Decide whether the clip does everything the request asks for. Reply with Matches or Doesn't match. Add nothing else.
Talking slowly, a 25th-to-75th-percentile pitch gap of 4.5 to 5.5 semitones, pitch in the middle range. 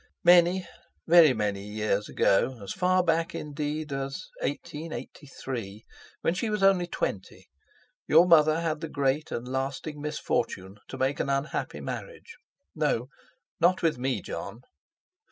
Matches